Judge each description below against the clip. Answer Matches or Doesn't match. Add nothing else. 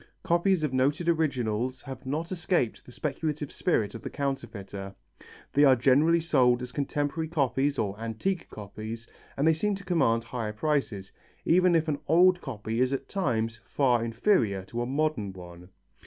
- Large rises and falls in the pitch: Matches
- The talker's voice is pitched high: Doesn't match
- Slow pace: Doesn't match